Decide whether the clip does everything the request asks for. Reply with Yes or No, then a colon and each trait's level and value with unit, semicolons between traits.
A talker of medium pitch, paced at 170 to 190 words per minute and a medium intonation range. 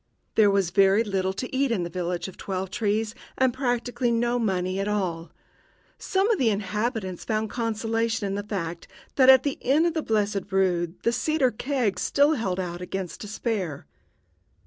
No: high, 210 Hz; average, 175 wpm; average, 4.3 semitones